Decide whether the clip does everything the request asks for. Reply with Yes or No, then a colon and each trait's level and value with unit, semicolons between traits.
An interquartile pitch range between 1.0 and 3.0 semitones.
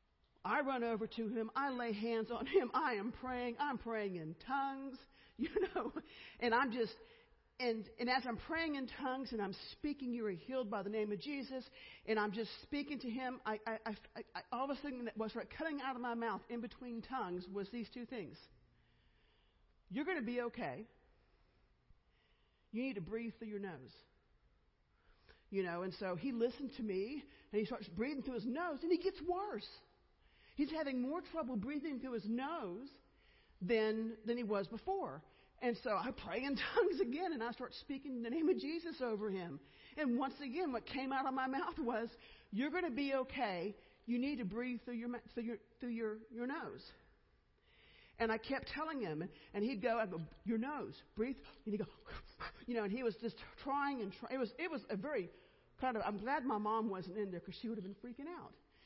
No: average, 3.8 semitones